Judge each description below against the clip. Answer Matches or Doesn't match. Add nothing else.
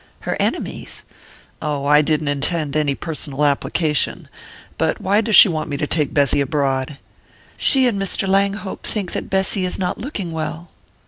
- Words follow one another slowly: Doesn't match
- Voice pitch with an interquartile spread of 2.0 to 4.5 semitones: Doesn't match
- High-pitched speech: Doesn't match